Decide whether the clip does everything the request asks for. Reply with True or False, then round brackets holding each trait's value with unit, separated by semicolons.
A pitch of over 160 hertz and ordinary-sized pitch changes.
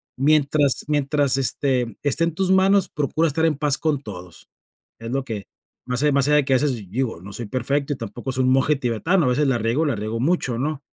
False (135 Hz; 3.3 semitones)